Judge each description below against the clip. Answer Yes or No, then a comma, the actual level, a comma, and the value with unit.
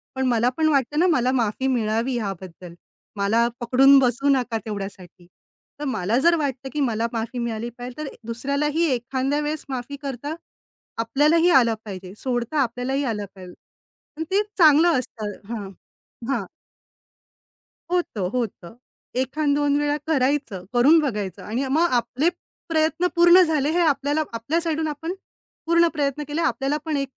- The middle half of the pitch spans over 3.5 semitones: Yes, average, 4.6 semitones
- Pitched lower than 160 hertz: No, very high, 265 Hz